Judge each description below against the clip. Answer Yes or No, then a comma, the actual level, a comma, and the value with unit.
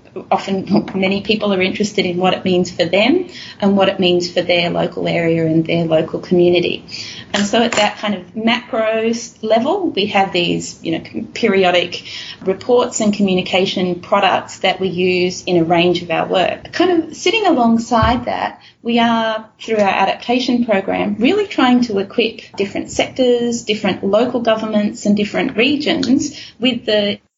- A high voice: Yes, high, 210 Hz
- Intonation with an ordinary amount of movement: Yes, average, 4.2 semitones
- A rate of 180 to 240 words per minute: No, average, 165 wpm